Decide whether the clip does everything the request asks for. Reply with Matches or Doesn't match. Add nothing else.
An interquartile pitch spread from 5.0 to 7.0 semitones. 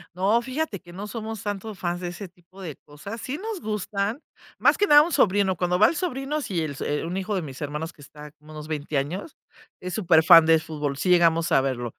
Matches